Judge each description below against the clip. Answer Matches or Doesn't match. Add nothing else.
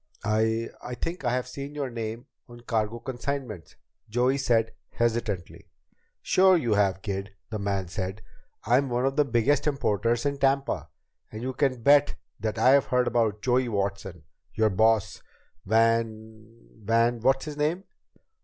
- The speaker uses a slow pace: Doesn't match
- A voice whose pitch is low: Matches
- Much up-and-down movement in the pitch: Doesn't match